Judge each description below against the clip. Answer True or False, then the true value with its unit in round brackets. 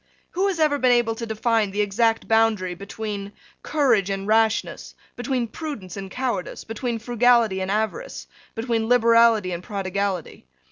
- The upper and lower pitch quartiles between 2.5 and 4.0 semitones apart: True (3.3 semitones)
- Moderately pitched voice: False (225 Hz)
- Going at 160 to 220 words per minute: False (145 wpm)